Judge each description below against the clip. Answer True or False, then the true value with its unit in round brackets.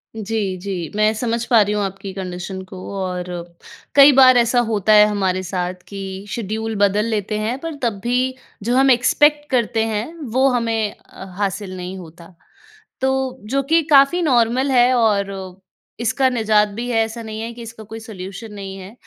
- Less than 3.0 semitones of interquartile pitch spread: False (3.8 semitones)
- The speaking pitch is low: False (220 Hz)